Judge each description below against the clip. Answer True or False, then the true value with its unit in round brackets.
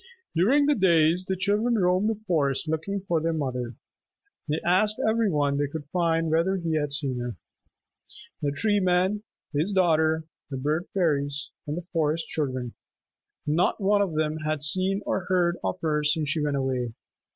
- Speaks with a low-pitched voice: False (160 Hz)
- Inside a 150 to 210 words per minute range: True (175 wpm)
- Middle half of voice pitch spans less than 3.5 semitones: False (4.2 semitones)